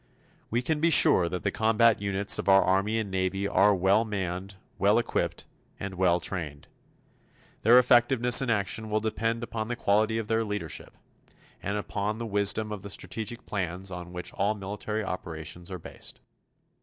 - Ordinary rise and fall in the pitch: Yes, average, 3.0 semitones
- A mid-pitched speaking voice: No, low, 100 Hz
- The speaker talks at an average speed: Yes, average, 170 wpm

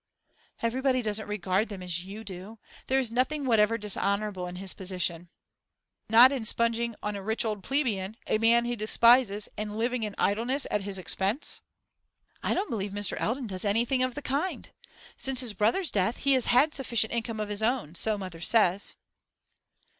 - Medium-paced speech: Yes, average, 180 wpm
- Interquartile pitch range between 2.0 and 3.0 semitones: No, average, 3.5 semitones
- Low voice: No, high, 220 Hz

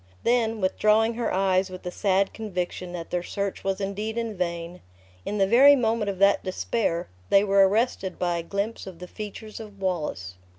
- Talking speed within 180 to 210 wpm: Yes, average, 185 wpm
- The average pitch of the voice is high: Yes, high, 195 Hz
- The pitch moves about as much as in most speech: Yes, average, 3.1 semitones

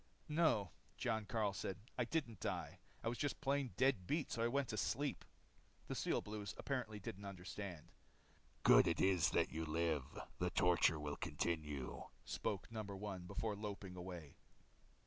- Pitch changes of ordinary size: Yes, average, 4.6 semitones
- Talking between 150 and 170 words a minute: Yes, average, 160 wpm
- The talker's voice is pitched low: Yes, low, 100 Hz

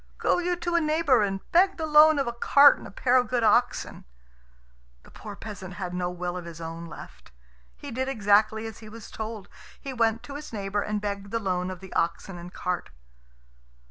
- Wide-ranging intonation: Yes, wide, 5.7 semitones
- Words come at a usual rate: No, fast, 210 wpm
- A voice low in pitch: No, high, 215 Hz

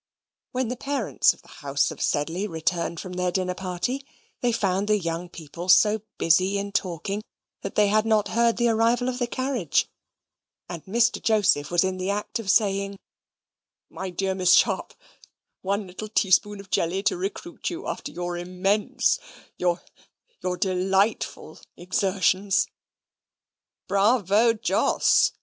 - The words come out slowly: No, average, 145 wpm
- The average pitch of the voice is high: Yes, high, 195 Hz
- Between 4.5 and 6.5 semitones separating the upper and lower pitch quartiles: No, average, 3.1 semitones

